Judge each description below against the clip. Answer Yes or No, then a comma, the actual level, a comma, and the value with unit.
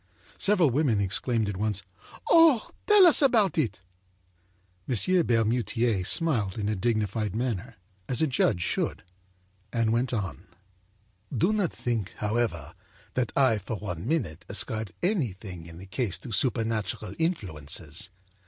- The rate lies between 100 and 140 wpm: Yes, slow, 135 wpm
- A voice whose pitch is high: No, low, 110 Hz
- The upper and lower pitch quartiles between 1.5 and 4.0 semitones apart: No, wide, 5.5 semitones